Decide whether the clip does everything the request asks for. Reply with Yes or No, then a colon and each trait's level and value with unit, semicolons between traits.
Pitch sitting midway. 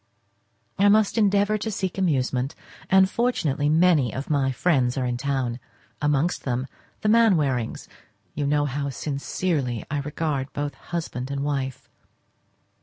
Yes: medium, 145 Hz